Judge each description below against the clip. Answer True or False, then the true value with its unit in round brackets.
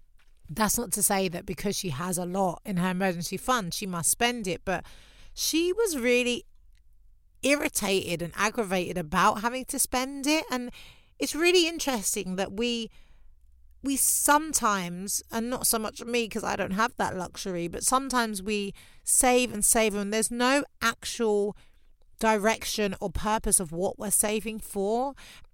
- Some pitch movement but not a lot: True (4.3 semitones)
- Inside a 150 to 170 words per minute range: True (155 wpm)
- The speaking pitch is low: False (215 Hz)